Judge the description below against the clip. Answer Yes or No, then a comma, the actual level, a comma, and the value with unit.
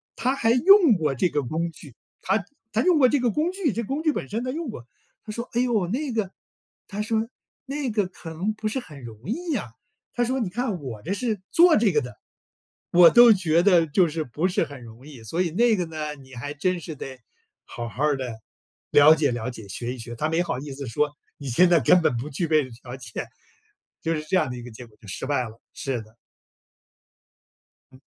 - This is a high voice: No, medium, 165 Hz